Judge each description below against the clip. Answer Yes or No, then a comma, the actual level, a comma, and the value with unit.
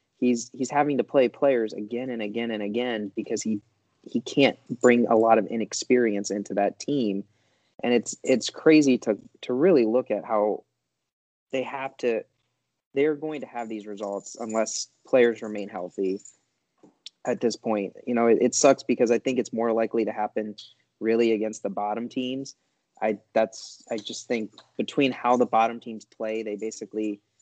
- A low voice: Yes, low, 115 Hz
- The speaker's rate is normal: Yes, average, 175 wpm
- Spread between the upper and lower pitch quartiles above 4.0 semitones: No, average, 2.7 semitones